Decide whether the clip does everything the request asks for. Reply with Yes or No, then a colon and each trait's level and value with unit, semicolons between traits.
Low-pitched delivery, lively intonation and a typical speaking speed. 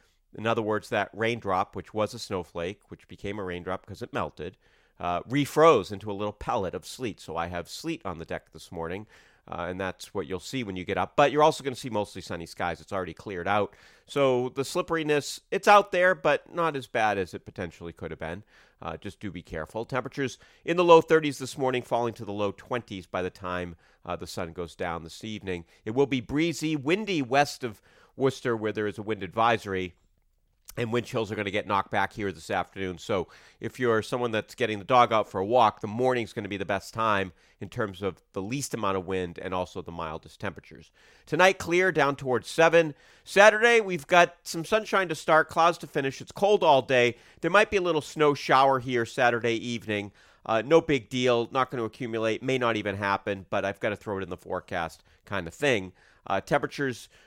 No: low, 115 Hz; wide, 6.4 semitones; fast, 225 wpm